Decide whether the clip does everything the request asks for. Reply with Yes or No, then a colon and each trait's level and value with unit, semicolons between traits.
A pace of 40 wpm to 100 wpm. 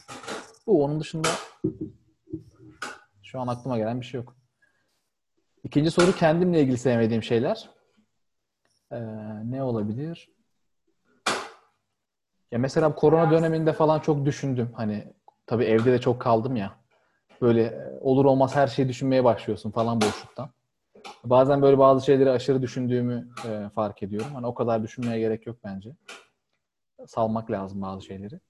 No: average, 130 wpm